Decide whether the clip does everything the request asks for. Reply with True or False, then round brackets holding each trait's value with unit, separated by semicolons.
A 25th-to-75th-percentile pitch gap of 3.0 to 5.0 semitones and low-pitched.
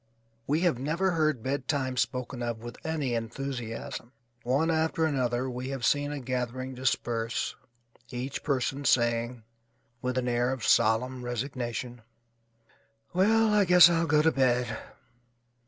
True (3.6 semitones; 130 Hz)